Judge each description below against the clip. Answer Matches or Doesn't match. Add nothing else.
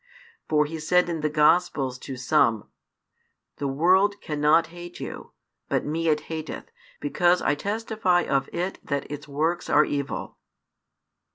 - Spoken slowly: Doesn't match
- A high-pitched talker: Doesn't match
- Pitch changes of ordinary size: Matches